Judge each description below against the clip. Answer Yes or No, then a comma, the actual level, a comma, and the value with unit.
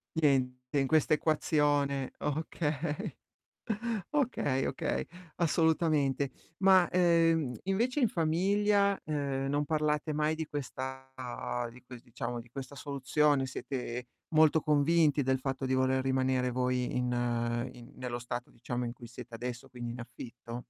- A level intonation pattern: No, average, 3.8 semitones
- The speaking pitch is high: No, low, 135 Hz